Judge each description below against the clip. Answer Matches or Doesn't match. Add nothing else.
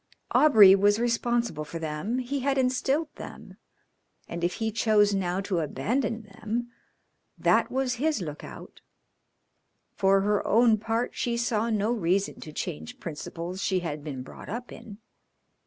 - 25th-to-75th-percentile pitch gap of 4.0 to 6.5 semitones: Matches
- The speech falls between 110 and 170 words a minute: Matches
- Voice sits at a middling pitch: Doesn't match